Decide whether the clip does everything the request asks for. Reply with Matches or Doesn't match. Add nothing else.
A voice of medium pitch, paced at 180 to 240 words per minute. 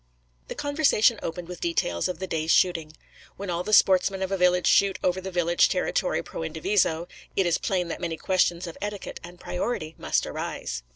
Matches